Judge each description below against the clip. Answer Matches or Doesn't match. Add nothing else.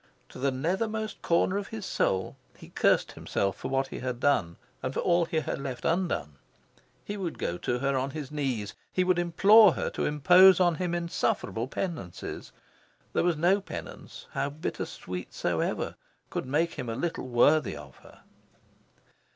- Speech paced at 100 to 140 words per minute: Doesn't match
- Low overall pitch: Doesn't match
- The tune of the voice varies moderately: Doesn't match